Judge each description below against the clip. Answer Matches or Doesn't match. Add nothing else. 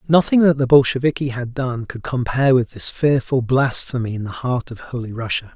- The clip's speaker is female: Doesn't match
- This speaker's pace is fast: Doesn't match